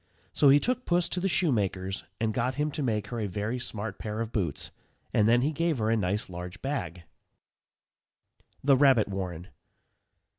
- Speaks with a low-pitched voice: Yes, low, 110 Hz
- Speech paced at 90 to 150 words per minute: No, average, 180 wpm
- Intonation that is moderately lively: No, wide, 6.0 semitones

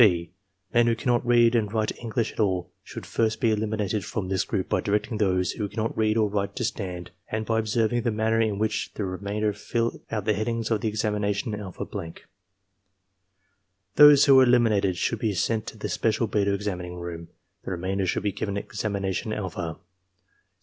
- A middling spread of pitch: No, narrow, 2.3 semitones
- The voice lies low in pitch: Yes, low, 105 Hz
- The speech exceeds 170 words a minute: Yes, average, 190 wpm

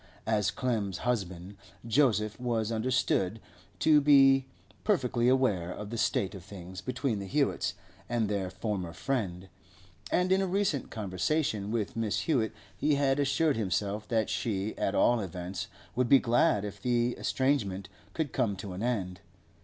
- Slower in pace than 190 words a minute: Yes, average, 155 wpm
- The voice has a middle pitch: No, low, 110 Hz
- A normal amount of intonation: Yes, average, 4.9 semitones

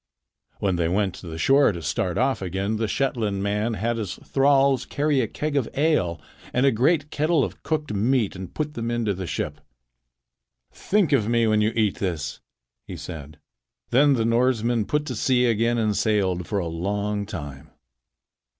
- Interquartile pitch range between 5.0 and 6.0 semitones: Yes, wide, 5.6 semitones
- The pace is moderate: Yes, average, 180 wpm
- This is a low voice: Yes, low, 110 Hz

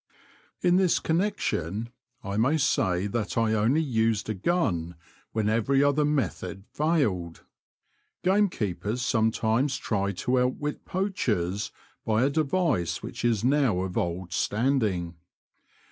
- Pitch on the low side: Yes, low, 115 Hz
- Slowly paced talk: Yes, slow, 125 wpm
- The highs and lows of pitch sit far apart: Yes, wide, 6.7 semitones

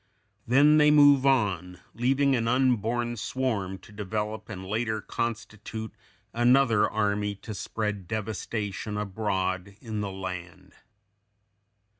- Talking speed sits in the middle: No, slow, 110 wpm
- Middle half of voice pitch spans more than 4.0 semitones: No, average, 3.3 semitones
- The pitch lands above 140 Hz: No, low, 110 Hz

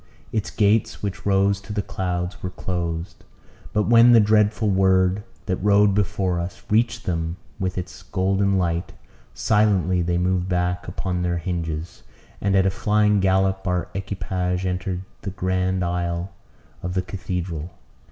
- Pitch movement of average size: No, narrow, 2.1 semitones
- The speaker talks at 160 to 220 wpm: No, average, 150 wpm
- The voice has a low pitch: Yes, very low, 95 Hz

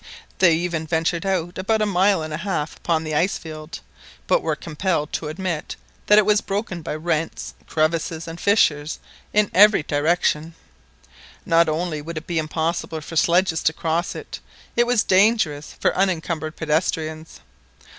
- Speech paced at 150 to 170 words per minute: Yes, average, 160 wpm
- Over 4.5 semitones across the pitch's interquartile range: No, average, 3.1 semitones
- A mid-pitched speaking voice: Yes, medium, 165 Hz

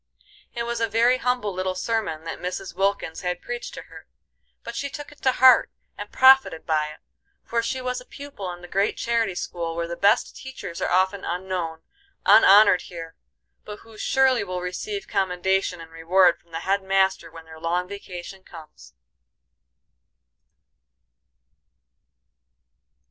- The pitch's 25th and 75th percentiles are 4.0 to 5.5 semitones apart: Yes, average, 4.9 semitones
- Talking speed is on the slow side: No, average, 155 wpm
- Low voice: No, high, 190 Hz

